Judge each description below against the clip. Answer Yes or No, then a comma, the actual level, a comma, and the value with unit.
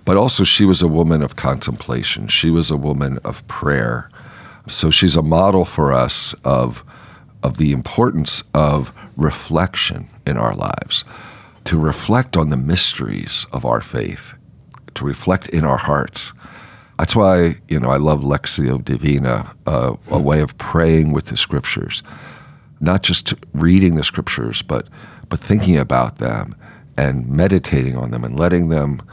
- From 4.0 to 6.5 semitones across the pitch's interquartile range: Yes, average, 4.8 semitones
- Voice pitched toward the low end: Yes, very low, 80 Hz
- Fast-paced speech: No, average, 155 wpm